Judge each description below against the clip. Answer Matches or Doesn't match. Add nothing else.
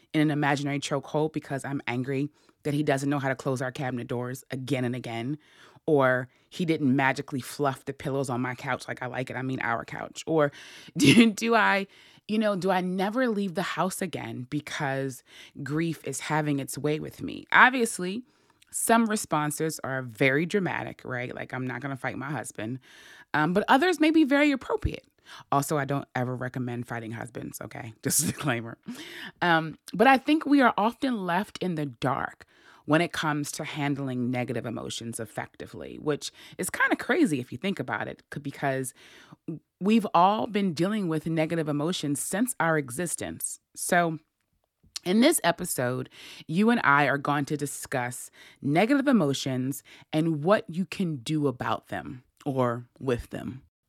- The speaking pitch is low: Doesn't match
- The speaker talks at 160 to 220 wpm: Matches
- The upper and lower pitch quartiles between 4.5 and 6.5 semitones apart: Matches